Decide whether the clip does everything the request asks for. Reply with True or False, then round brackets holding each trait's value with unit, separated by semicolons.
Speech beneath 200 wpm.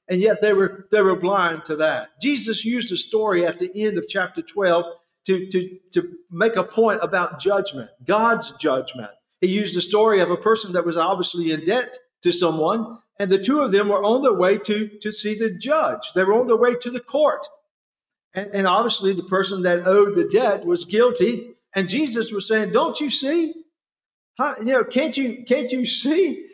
False (205 wpm)